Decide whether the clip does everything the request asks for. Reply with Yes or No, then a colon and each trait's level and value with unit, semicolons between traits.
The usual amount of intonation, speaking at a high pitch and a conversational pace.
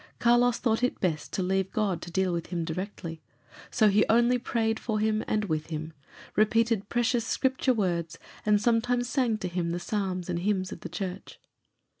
Yes: average, 4.4 semitones; high, 205 Hz; average, 185 wpm